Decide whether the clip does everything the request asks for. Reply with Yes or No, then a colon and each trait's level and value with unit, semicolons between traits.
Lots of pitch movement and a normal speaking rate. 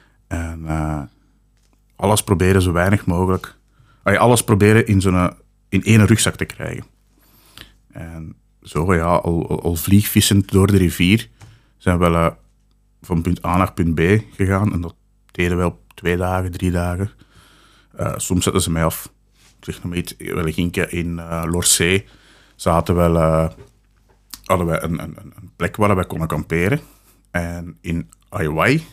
No: average, 3.4 semitones; average, 155 wpm